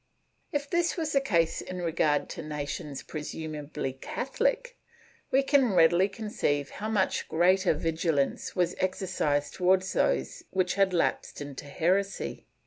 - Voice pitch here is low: No, medium, 180 Hz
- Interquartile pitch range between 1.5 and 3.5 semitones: No, average, 5.1 semitones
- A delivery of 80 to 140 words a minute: Yes, slow, 135 wpm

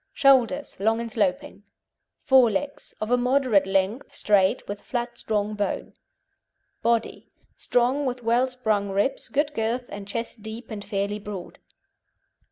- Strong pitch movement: No, average, 3.6 semitones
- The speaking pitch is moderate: No, high, 225 Hz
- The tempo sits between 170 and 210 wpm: No, average, 140 wpm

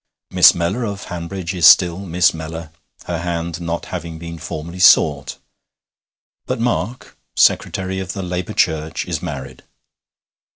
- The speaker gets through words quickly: No, slow, 135 wpm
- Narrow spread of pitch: Yes, narrow, 2.0 semitones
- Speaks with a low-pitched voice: Yes, very low, 85 Hz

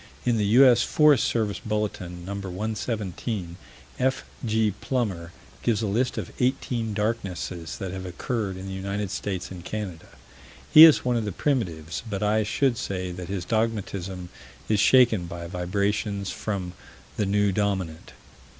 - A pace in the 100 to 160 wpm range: Yes, average, 150 wpm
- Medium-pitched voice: No, low, 100 Hz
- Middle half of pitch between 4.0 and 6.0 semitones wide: No, average, 3.6 semitones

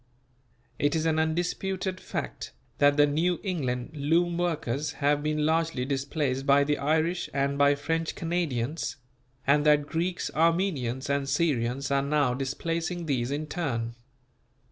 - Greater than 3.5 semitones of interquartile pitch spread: No, average, 3.0 semitones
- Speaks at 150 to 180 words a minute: No, average, 140 wpm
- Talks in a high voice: No, medium, 150 Hz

